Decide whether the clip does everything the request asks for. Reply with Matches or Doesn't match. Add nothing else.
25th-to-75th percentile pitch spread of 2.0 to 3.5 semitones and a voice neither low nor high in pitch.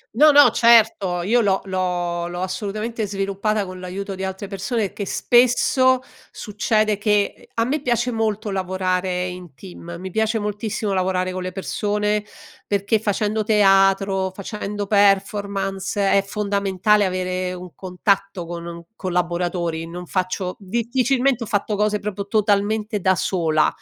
Doesn't match